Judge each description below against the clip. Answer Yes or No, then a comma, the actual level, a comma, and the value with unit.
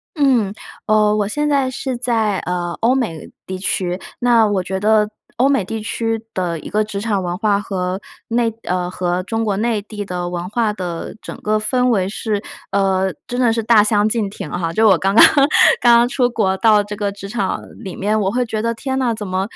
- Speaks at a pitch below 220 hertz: Yes, high, 210 Hz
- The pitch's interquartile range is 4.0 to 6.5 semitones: No, average, 3.3 semitones